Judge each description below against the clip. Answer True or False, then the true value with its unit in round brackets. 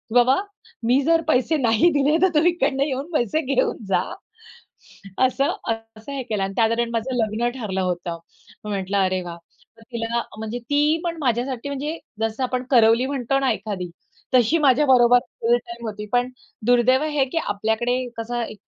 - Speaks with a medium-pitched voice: False (245 Hz)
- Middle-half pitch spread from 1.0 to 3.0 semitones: False (3.7 semitones)